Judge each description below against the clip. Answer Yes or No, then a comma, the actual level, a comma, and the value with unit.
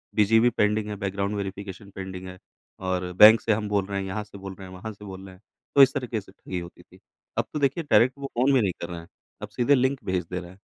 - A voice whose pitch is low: Yes, low, 100 Hz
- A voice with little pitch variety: No, average, 3.0 semitones